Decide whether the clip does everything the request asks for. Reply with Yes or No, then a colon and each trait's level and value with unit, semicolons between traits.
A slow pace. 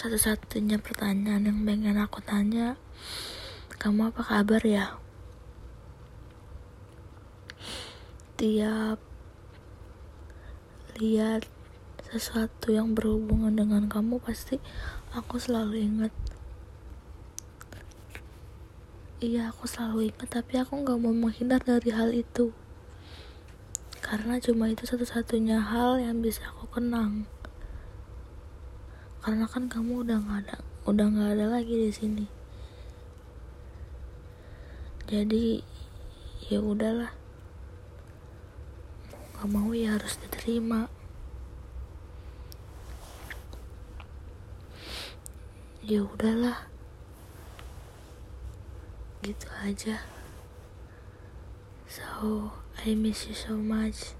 Yes: slow, 80 wpm